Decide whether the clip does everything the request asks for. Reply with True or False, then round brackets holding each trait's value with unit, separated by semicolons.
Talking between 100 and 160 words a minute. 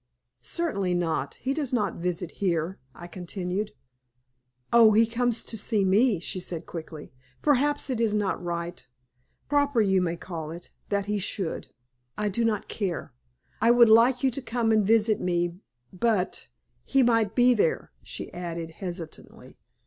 True (155 wpm)